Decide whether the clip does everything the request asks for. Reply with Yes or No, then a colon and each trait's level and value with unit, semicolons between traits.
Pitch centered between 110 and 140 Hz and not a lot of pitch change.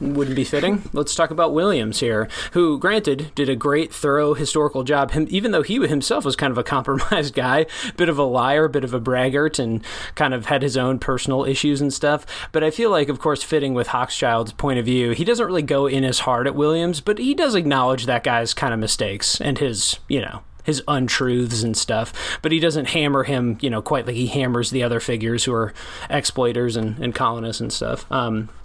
No: low, 135 Hz; average, 3.6 semitones